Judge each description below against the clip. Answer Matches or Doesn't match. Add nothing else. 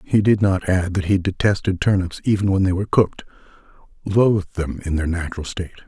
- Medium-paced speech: Matches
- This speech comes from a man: Matches